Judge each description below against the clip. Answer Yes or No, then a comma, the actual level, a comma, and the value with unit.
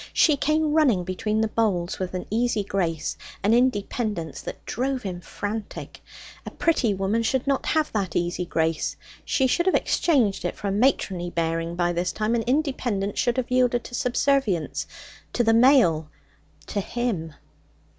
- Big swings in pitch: Yes, wide, 5.8 semitones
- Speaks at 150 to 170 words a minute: Yes, average, 165 wpm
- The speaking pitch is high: Yes, high, 220 Hz